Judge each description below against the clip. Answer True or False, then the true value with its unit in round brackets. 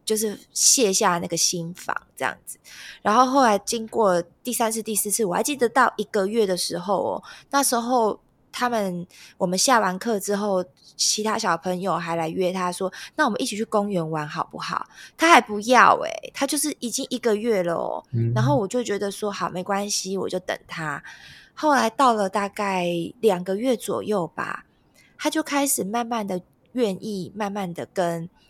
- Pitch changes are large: False (4.6 semitones)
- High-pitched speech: True (205 Hz)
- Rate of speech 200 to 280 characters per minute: True (260 characters per minute)